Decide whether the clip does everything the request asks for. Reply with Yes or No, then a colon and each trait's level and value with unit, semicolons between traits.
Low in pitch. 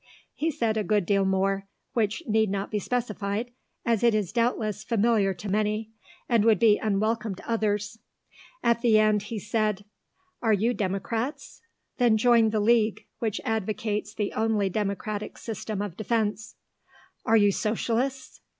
No: high, 215 Hz